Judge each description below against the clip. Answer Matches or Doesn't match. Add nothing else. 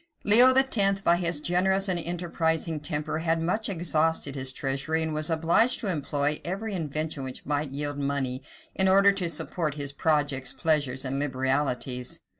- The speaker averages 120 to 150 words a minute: Doesn't match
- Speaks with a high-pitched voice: Doesn't match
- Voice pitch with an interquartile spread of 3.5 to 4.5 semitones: Matches